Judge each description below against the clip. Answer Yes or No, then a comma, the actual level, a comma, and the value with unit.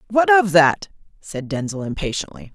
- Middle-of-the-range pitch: Yes, medium, 170 Hz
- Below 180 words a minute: Yes, average, 140 wpm